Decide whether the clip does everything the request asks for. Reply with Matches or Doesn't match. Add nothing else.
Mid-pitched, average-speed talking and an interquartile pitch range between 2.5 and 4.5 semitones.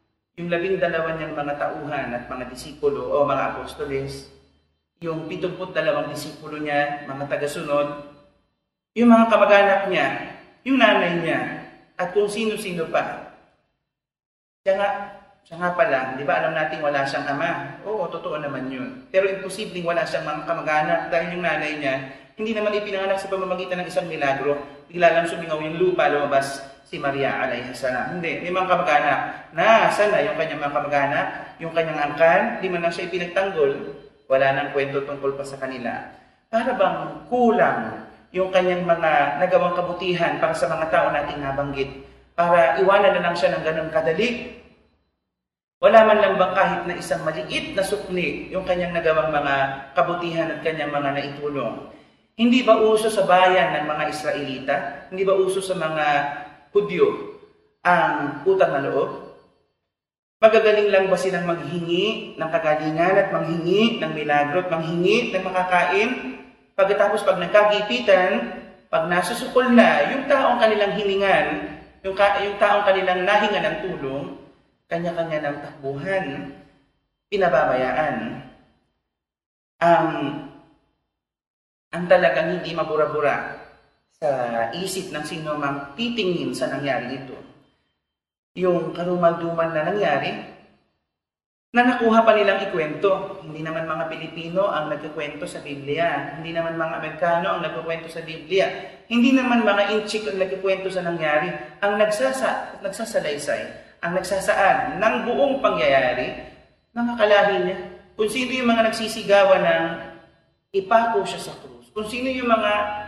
Doesn't match